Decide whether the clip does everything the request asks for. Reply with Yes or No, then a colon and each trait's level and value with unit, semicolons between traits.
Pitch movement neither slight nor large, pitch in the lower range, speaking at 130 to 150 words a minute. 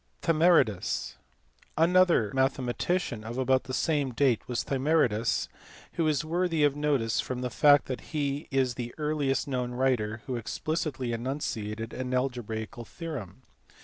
Yes: average, 3.9 semitones; low, 130 Hz; slow, 135 wpm